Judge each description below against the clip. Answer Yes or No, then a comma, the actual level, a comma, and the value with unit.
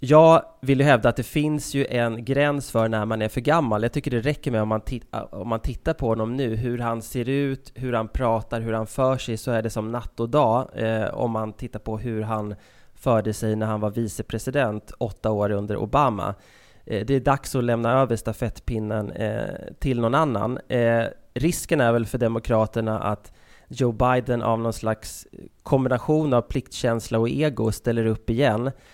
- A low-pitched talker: Yes, low, 115 Hz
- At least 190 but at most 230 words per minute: Yes, average, 200 wpm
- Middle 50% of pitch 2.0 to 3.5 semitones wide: Yes, average, 3.0 semitones